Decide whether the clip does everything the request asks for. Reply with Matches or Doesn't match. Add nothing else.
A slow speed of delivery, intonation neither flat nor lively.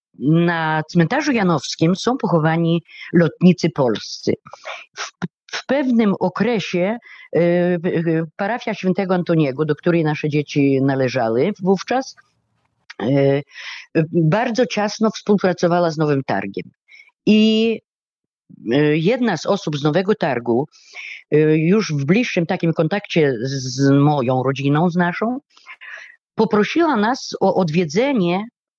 Doesn't match